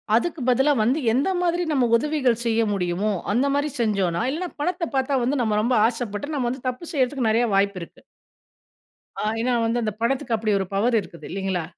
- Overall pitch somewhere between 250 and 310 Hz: No, high, 240 Hz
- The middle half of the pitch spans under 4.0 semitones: No, average, 4.4 semitones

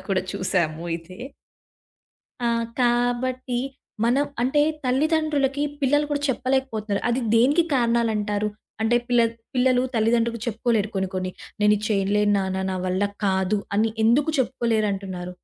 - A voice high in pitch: Yes, high, 230 Hz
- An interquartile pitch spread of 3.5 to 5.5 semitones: Yes, average, 4.2 semitones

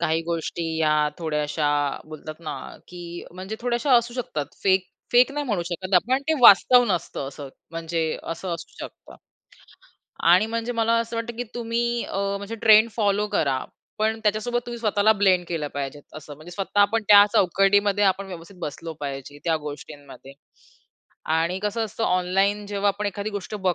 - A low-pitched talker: No, high, 195 Hz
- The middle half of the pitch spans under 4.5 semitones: No, average, 5.1 semitones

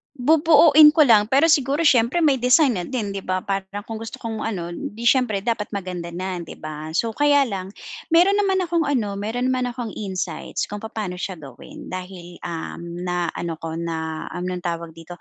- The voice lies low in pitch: No, high, 210 Hz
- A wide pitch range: Yes, wide, 6.8 semitones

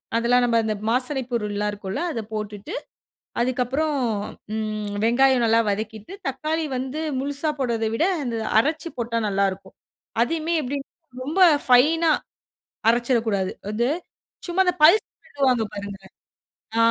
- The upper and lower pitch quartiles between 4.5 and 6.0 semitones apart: Yes, average, 4.9 semitones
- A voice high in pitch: Yes, high, 240 Hz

